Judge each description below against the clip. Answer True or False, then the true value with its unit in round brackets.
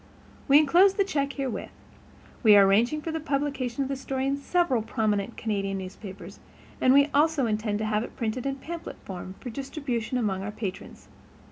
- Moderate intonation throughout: True (5.0 semitones)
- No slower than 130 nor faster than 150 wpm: False (180 wpm)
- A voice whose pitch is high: True (255 Hz)